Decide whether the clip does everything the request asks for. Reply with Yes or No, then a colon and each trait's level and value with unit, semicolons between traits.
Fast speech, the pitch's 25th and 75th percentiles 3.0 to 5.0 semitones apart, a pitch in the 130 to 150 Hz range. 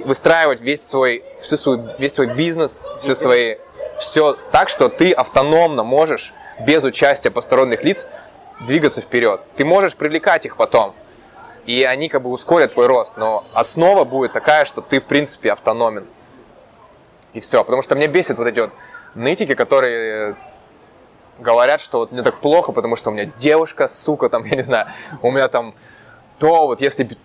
Yes: fast, 165 wpm; average, 4.2 semitones; medium, 140 Hz